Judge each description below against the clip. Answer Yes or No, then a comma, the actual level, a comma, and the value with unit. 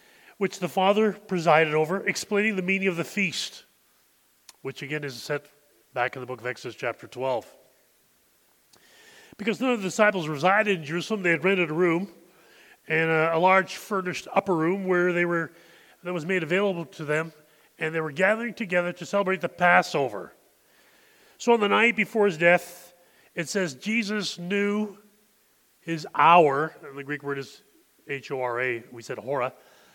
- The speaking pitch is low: No, medium, 175 Hz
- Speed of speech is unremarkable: Yes, average, 170 wpm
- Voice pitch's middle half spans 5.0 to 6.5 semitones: No, average, 4.4 semitones